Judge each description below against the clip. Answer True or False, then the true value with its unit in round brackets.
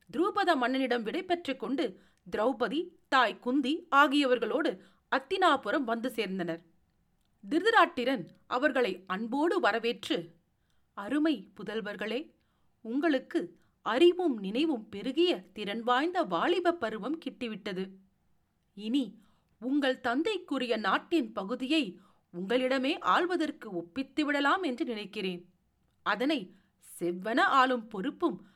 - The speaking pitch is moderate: False (255 Hz)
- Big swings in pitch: True (6.7 semitones)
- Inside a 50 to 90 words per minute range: True (85 wpm)